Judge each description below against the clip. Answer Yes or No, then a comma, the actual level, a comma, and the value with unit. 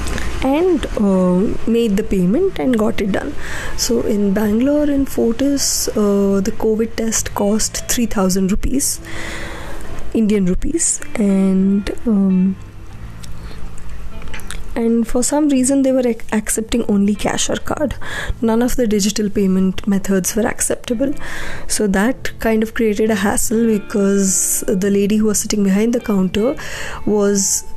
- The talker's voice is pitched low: No, high, 215 Hz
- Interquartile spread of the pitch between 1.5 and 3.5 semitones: Yes, average, 3.2 semitones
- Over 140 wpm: No, slow, 135 wpm